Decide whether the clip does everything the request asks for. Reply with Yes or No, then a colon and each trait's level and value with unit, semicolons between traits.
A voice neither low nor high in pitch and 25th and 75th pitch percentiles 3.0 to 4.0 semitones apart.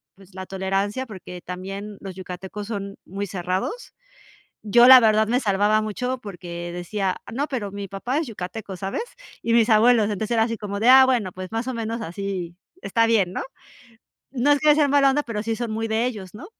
No: high, 210 Hz; average, 3.6 semitones